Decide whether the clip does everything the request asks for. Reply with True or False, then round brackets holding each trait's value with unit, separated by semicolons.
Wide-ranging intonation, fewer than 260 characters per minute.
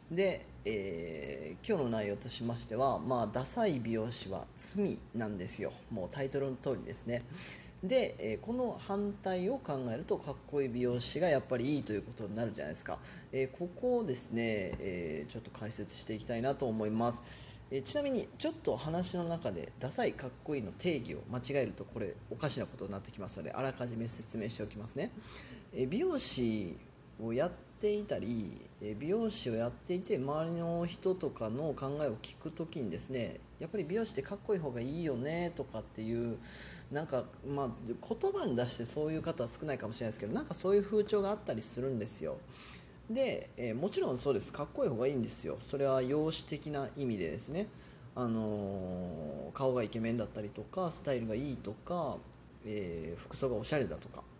False (6.8 semitones; 395 characters per minute)